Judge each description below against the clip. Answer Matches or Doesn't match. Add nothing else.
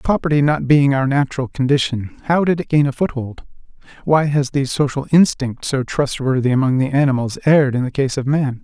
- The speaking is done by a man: Matches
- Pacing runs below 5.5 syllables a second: Doesn't match